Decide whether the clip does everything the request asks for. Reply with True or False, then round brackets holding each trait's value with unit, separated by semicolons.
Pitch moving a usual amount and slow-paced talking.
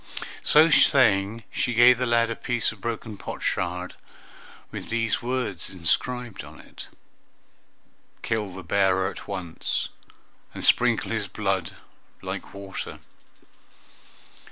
True (3.9 semitones; 115 wpm)